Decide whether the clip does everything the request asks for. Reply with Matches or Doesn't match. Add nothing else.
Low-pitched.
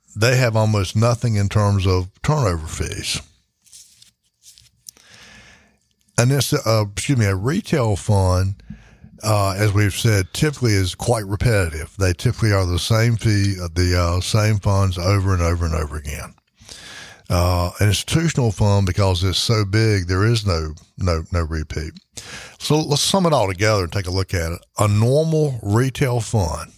Matches